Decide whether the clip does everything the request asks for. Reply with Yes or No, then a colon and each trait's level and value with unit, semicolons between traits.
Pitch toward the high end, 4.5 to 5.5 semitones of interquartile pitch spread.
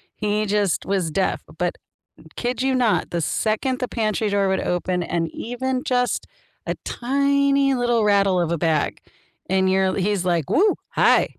Yes: high, 210 Hz; average, 5.1 semitones